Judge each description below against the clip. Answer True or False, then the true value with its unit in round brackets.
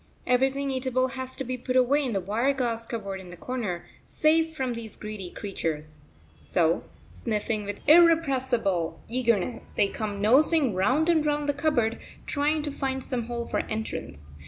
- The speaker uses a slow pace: False (170 wpm)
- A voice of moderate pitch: False (245 Hz)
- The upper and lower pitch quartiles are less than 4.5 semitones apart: False (5.1 semitones)